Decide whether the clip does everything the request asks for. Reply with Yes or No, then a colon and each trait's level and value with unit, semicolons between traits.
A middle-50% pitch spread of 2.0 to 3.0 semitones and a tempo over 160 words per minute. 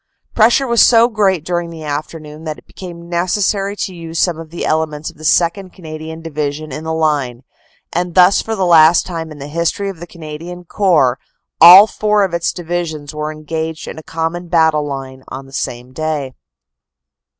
Yes: narrow, 2.6 semitones; average, 185 wpm